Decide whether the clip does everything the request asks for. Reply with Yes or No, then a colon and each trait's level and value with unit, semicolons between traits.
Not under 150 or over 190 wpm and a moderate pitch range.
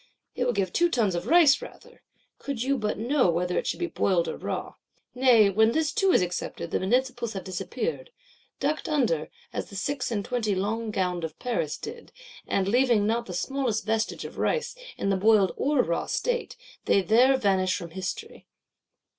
No: average, 180 wpm; wide, 5.9 semitones